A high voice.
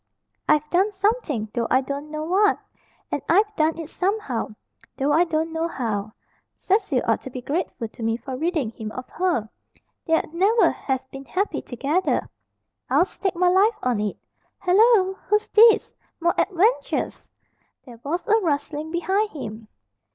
Yes: very high, 325 Hz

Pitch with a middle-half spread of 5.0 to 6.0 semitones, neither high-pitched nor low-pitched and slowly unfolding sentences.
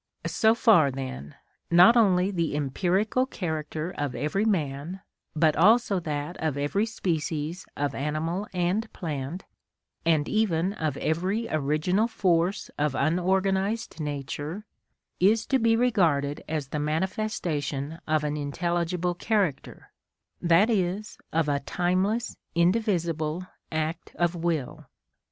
No: average, 4.5 semitones; medium, 170 Hz; slow, 120 wpm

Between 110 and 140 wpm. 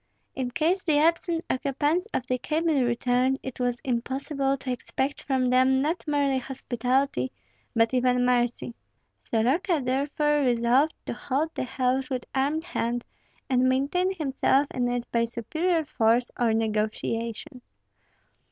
Yes: slow, 135 wpm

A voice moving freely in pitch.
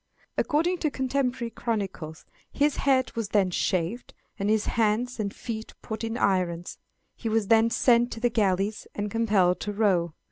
No: average, 3.5 semitones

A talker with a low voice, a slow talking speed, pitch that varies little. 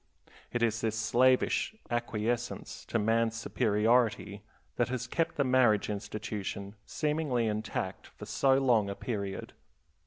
No: low, 115 Hz; slow, 125 wpm; average, 3.0 semitones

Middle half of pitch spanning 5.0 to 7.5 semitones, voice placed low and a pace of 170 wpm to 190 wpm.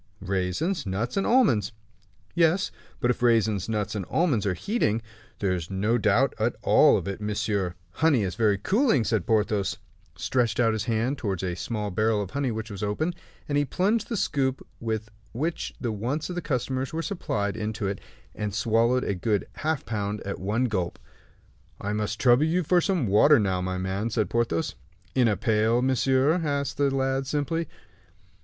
Yes: average, 5.3 semitones; low, 115 Hz; average, 185 wpm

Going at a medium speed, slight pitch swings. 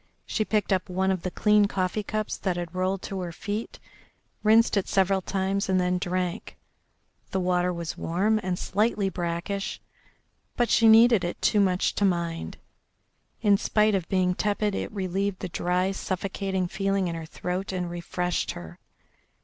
Yes: average, 165 wpm; narrow, 2.1 semitones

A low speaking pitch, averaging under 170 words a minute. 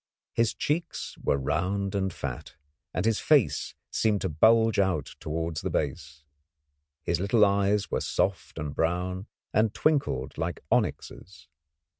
Yes: very low, 95 Hz; slow, 135 wpm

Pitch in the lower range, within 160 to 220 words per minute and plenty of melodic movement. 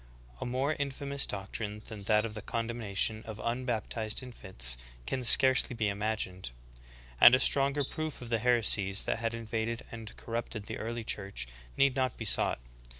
No: low, 115 Hz; average, 170 wpm; average, 3.1 semitones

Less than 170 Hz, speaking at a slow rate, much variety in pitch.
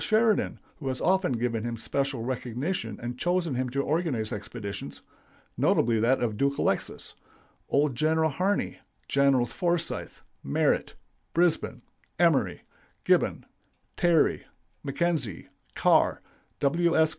Yes: medium, 140 Hz; slow, 120 wpm; wide, 5.9 semitones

